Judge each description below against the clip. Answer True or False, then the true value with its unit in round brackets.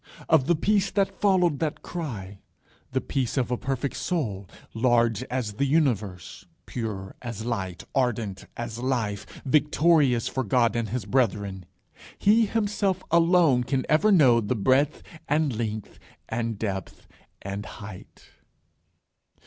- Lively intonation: True (6.1 semitones)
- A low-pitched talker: True (125 Hz)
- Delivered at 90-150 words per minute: True (135 wpm)